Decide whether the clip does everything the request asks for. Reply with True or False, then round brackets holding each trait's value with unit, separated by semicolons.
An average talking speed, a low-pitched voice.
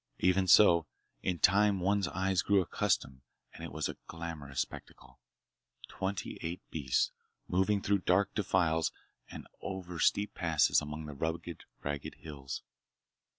False (130 wpm; 85 Hz)